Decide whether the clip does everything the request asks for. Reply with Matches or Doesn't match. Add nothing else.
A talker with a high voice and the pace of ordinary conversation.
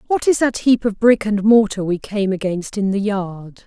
Doesn't match